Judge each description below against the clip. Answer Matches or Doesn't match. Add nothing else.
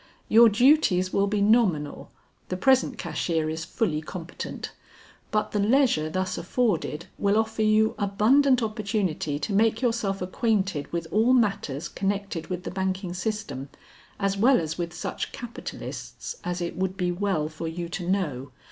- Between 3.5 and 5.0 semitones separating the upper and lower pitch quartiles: Matches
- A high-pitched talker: Matches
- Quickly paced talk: Doesn't match